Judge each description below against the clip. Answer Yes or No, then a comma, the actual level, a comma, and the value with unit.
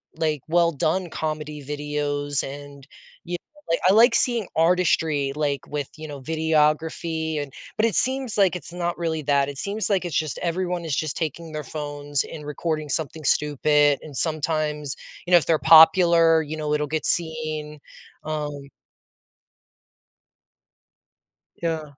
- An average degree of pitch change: No, narrow, 2.3 semitones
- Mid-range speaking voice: Yes, medium, 155 Hz